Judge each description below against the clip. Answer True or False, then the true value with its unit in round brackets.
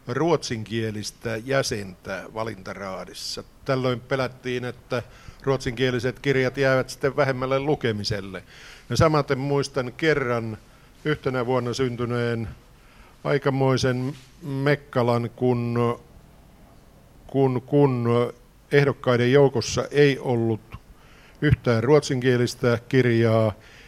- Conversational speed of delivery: False (80 wpm)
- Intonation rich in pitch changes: False (2.5 semitones)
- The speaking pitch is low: True (125 Hz)